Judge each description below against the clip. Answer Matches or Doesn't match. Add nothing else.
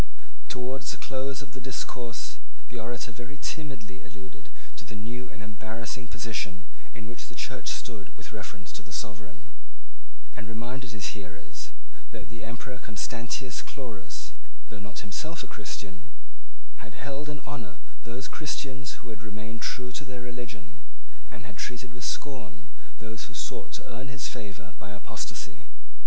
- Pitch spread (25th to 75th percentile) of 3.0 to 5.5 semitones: Matches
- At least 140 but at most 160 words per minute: Matches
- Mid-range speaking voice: Doesn't match